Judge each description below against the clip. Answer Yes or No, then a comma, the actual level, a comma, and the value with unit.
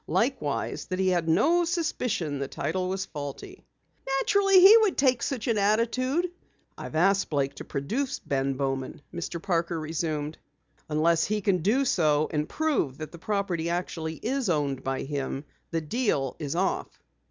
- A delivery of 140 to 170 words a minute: Yes, average, 160 wpm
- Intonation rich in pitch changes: Yes, wide, 7.7 semitones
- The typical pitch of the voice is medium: Yes, medium, 170 Hz